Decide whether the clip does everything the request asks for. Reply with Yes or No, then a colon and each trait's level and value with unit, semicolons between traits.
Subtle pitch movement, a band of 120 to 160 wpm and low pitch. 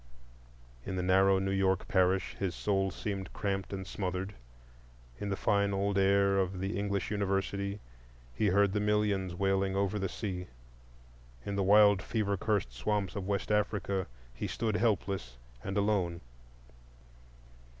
Yes: narrow, 1.2 semitones; average, 145 wpm; low, 100 Hz